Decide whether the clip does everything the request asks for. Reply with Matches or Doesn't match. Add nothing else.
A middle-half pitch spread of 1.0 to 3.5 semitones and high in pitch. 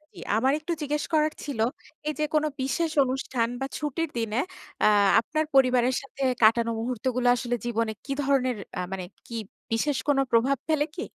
Doesn't match